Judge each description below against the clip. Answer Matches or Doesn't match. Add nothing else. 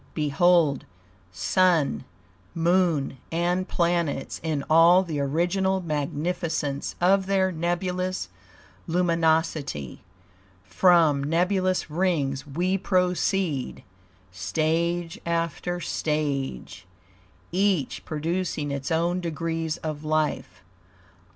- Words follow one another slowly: Matches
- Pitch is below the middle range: Doesn't match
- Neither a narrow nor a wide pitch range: Matches